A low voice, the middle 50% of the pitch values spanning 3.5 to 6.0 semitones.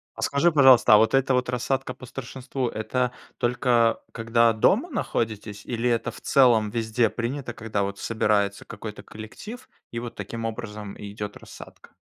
No: low, 115 Hz; average, 2.7 semitones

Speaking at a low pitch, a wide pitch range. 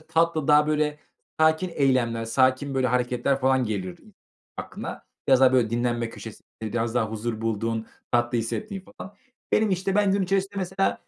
Yes: low, 130 Hz; wide, 5.9 semitones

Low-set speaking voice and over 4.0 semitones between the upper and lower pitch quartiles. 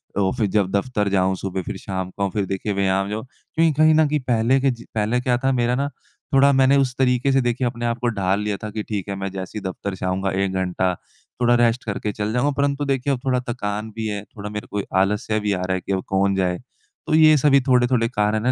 Yes: low, 110 Hz; average, 4.5 semitones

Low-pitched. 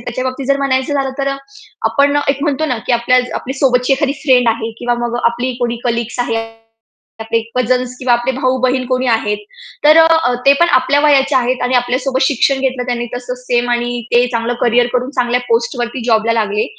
No: very high, 250 Hz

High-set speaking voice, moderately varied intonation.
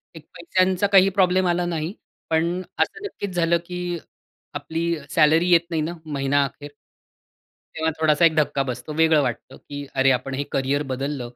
No: medium, 160 Hz; average, 3.5 semitones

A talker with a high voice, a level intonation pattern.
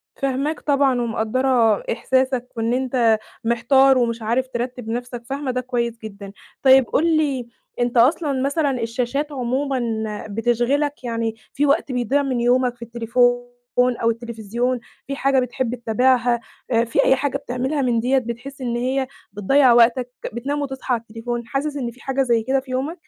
Yes: very high, 250 Hz; narrow, 2.3 semitones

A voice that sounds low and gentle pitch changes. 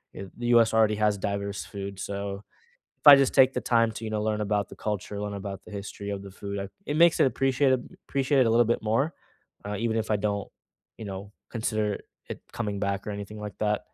Yes: low, 105 Hz; narrow, 2.3 semitones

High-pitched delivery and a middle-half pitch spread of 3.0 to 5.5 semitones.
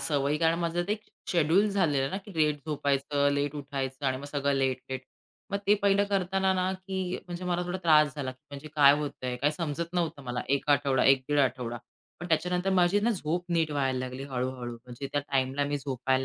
No: medium, 145 Hz; average, 4.6 semitones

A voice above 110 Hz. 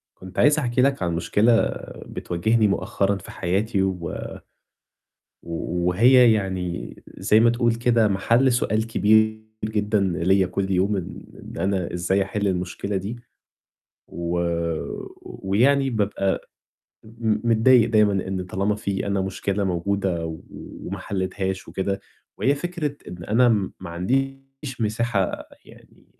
No: low, 100 Hz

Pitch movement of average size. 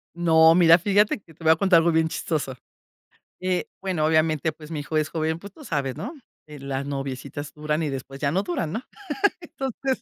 Yes: average, 3.1 semitones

